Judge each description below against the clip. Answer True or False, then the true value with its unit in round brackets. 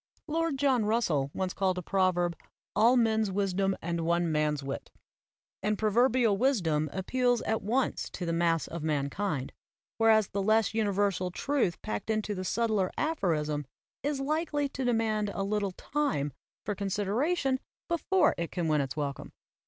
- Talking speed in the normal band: True (160 wpm)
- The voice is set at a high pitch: True (200 Hz)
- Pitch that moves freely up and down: True (5.7 semitones)